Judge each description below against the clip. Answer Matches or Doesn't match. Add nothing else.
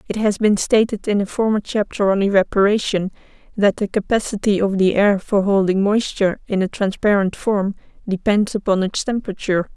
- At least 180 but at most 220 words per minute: Doesn't match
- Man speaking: Doesn't match